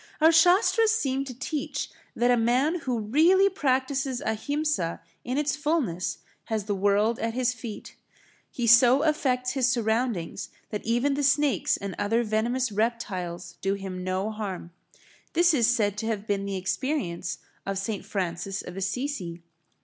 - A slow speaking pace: No, average, 155 wpm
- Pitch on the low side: No, high, 235 Hz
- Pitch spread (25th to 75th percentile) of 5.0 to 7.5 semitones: Yes, wide, 5.6 semitones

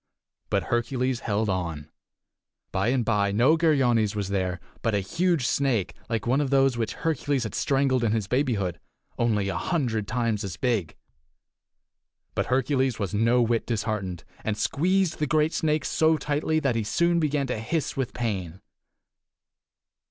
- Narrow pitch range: No, average, 5.2 semitones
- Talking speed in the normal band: Yes, average, 160 wpm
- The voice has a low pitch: Yes, low, 120 Hz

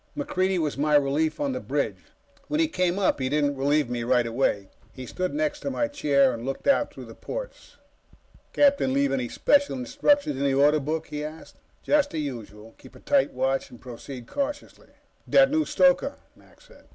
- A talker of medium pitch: Yes, medium, 150 Hz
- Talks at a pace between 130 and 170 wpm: No, average, 195 wpm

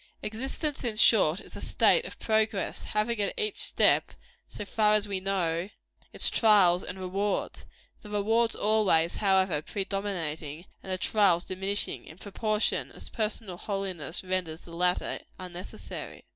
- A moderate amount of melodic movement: Yes, average, 3.0 semitones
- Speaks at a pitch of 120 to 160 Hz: No, high, 195 Hz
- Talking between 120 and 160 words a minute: Yes, average, 145 wpm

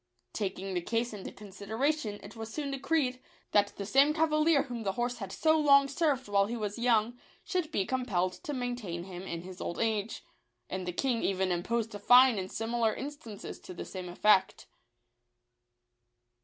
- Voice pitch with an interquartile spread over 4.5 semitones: Yes, average, 5.2 semitones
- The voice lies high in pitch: Yes, high, 225 Hz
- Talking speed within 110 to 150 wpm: No, average, 180 wpm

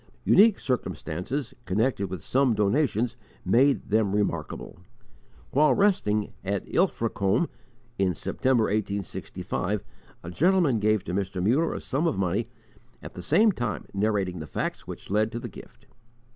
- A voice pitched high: No, low, 110 Hz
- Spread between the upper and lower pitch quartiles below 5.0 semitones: No, wide, 5.4 semitones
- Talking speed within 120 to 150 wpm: Yes, average, 140 wpm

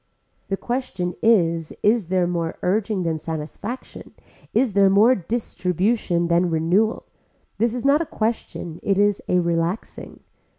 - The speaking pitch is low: No, high, 190 Hz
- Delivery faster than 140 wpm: No, slow, 135 wpm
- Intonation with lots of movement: No, average, 4.6 semitones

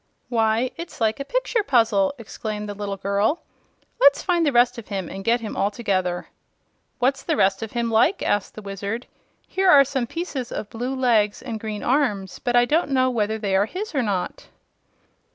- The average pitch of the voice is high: Yes, high, 230 Hz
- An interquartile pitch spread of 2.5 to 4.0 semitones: No, average, 4.6 semitones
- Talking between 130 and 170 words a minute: No, average, 195 wpm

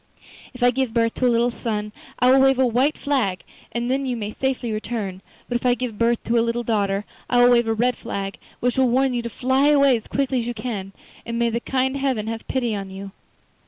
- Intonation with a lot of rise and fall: No, narrow, 2.5 semitones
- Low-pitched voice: No, high, 240 Hz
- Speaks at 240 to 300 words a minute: Yes, fast, 245 wpm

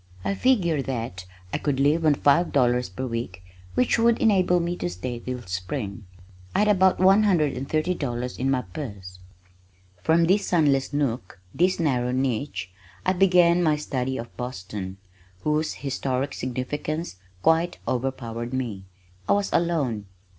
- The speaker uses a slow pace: No, average, 155 wpm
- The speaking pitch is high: No, low, 135 Hz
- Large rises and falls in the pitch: Yes, wide, 6.1 semitones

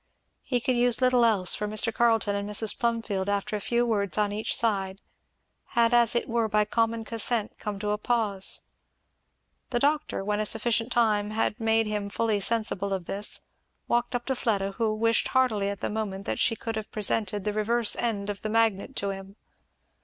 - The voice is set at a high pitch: Yes, high, 215 Hz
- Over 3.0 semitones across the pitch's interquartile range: No, narrow, 2.4 semitones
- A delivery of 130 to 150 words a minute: No, average, 195 wpm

